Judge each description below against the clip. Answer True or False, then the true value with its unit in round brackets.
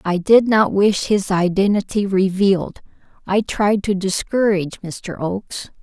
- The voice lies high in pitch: True (195 Hz)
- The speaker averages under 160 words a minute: True (135 wpm)